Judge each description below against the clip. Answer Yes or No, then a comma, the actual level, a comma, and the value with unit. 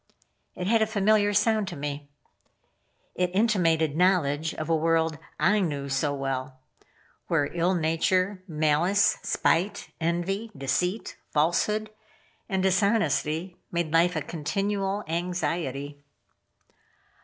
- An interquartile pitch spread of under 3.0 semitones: No, average, 4.2 semitones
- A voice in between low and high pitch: Yes, medium, 170 Hz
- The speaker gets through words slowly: Yes, slow, 110 wpm